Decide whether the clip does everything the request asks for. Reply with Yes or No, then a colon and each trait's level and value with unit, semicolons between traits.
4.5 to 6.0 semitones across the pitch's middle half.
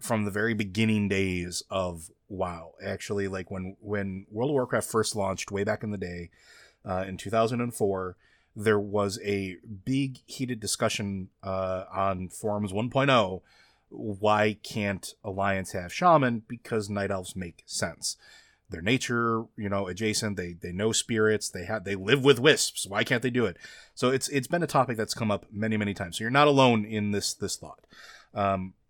No: average, 2.8 semitones